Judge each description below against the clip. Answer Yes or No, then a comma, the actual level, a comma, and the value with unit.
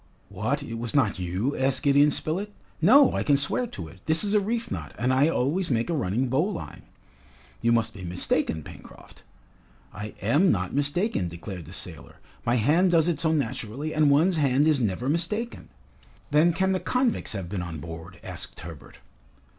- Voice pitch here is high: No, medium, 140 Hz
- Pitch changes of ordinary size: No, wide, 8.5 semitones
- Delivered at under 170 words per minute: No, average, 185 wpm